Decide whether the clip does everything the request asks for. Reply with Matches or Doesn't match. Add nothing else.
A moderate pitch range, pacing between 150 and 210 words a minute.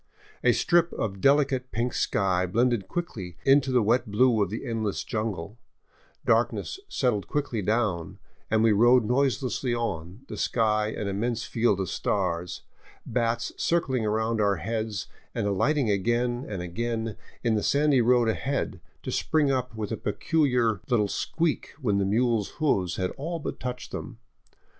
Matches